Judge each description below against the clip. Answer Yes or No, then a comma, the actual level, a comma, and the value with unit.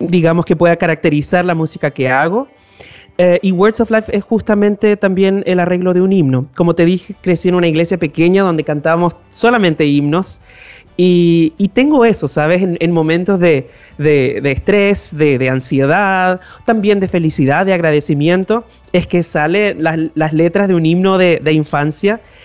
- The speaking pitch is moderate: Yes, medium, 175 Hz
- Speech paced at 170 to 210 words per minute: Yes, average, 175 wpm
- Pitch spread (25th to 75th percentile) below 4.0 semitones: Yes, average, 3.4 semitones